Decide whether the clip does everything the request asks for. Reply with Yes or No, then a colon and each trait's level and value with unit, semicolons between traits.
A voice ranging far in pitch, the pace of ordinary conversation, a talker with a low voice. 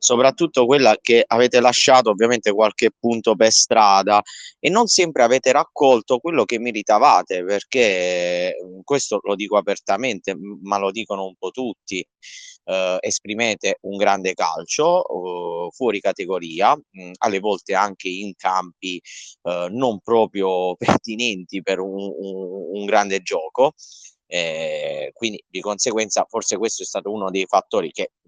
Yes: wide, 6.3 semitones; average, 140 wpm; low, 105 Hz